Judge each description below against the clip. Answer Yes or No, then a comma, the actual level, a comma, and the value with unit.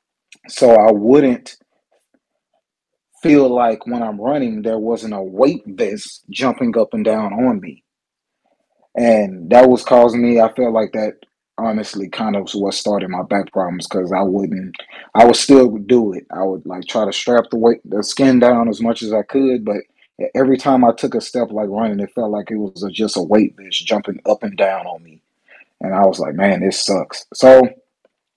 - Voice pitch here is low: Yes, low, 110 Hz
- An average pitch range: Yes, average, 3.4 semitones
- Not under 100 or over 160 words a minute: No, average, 200 wpm